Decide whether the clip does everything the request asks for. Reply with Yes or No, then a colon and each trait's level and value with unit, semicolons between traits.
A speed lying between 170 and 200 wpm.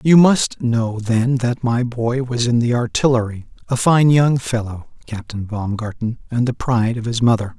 Yes: average, 175 wpm